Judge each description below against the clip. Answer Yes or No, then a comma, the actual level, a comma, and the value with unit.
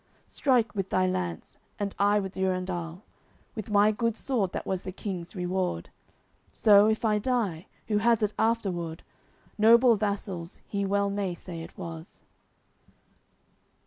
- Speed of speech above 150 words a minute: No, average, 145 wpm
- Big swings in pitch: No, average, 2.9 semitones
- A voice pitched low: No, high, 200 Hz